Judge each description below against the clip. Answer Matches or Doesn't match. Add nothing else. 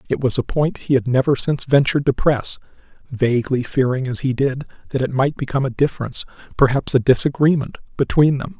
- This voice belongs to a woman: Doesn't match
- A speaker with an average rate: Matches